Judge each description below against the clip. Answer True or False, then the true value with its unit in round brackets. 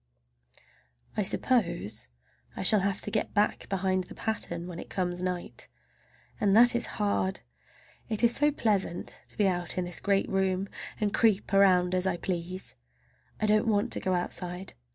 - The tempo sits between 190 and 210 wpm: False (170 wpm)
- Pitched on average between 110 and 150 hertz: False (190 Hz)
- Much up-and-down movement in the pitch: False (2.8 semitones)